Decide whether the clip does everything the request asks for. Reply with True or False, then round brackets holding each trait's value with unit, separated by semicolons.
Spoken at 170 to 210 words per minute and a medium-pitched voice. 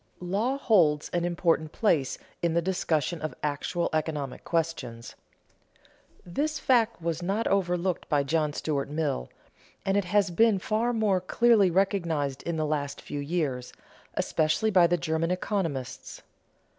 False (145 wpm; 170 Hz)